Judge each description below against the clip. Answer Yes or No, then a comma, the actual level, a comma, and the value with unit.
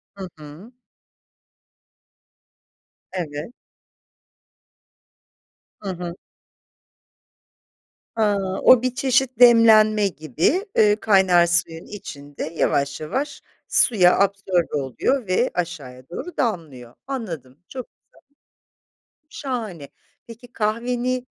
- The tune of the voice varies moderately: No, wide, 6.6 semitones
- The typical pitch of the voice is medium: No, high, 200 Hz